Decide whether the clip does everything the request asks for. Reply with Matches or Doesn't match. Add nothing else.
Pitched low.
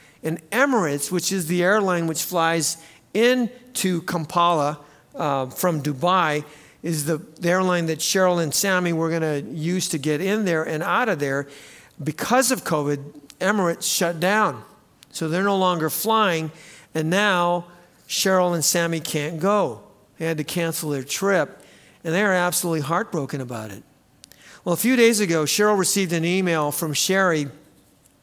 Doesn't match